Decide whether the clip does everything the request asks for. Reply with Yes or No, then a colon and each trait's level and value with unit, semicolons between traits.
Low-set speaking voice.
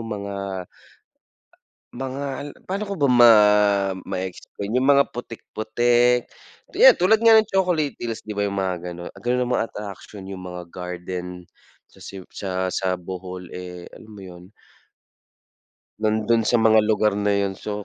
Yes: low, 105 Hz